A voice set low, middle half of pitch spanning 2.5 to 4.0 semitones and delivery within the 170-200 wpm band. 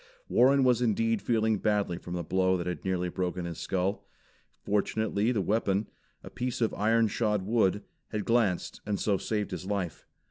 Yes: low, 105 Hz; average, 3.3 semitones; average, 175 wpm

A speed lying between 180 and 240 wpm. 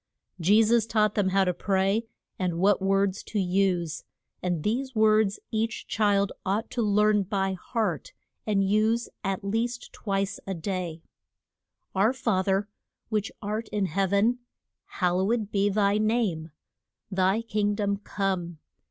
No: average, 150 wpm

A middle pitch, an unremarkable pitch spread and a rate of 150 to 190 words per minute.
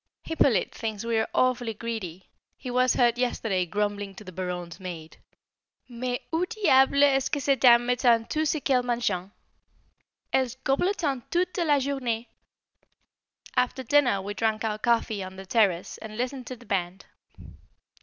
No: high, 235 Hz; average, 4.4 semitones; average, 155 wpm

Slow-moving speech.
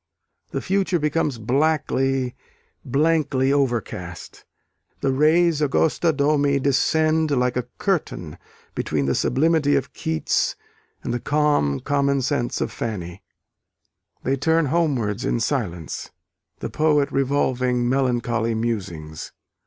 Yes: slow, 105 wpm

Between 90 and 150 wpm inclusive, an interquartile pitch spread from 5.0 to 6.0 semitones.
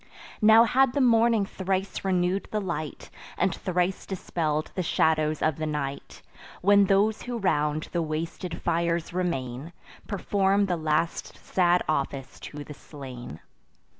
No: slow, 135 wpm; average, 4.2 semitones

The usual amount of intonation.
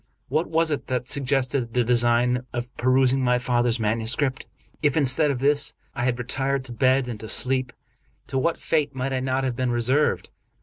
No: narrow, 2.0 semitones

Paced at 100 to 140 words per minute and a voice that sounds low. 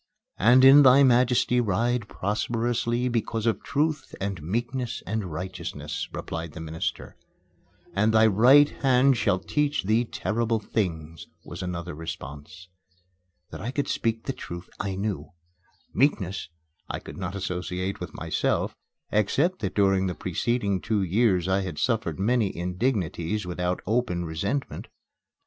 Yes: slow, 135 wpm; low, 105 Hz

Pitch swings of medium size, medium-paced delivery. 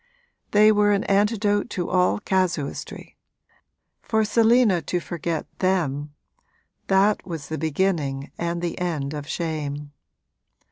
No: average, 4.9 semitones; slow, 120 wpm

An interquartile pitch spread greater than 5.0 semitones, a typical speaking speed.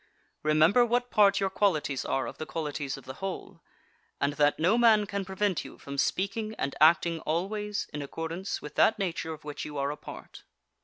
Yes: wide, 5.4 semitones; average, 195 wpm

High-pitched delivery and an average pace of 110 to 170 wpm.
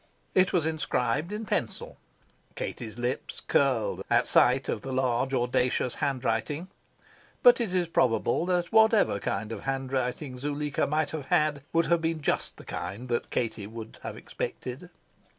No: low, 135 Hz; average, 150 wpm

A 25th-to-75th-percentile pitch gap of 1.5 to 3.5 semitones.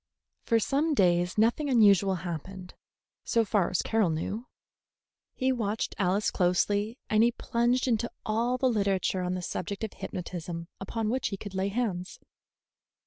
No: average, 4.2 semitones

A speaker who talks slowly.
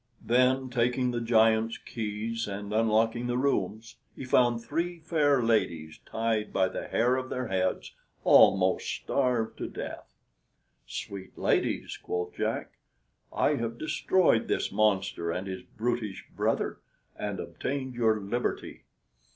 Yes: slow, 130 wpm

